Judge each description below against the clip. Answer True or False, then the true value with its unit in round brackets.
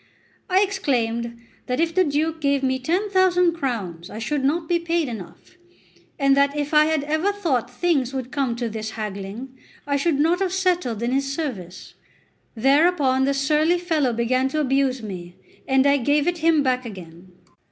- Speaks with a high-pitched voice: True (275 Hz)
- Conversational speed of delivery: True (180 wpm)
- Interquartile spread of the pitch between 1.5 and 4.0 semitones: False (5.2 semitones)